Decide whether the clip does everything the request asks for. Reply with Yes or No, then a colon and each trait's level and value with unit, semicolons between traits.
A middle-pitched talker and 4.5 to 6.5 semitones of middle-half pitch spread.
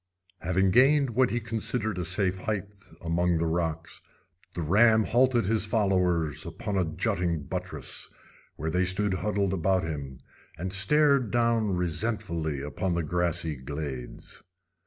No: very low, 95 Hz; average, 4.9 semitones